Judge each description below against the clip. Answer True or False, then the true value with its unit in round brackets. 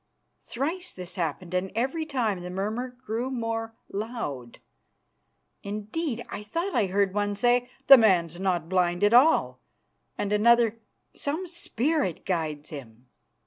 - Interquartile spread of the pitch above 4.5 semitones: True (5.3 semitones)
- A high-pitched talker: True (210 Hz)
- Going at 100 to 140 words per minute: True (135 wpm)